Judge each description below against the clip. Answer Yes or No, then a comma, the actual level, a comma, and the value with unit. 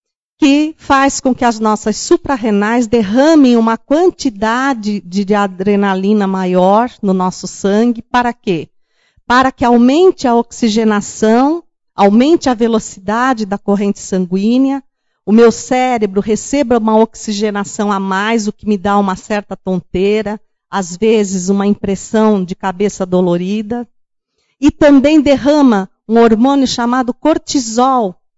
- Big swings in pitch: No, average, 4.2 semitones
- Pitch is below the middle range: No, high, 220 Hz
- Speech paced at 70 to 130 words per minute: Yes, average, 125 wpm